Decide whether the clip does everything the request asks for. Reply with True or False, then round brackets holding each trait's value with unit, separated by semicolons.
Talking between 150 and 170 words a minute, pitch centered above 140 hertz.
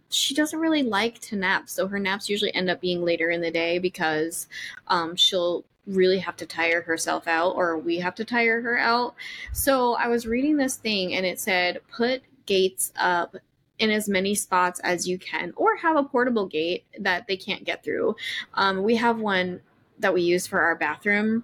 False (200 wpm; 190 Hz)